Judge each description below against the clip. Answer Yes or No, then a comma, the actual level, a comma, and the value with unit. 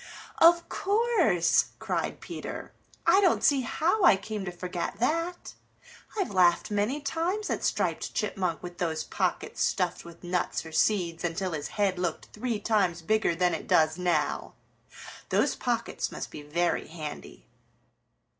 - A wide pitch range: Yes, wide, 7.6 semitones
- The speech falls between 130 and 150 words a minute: Yes, average, 145 wpm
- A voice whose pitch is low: No, medium, 185 Hz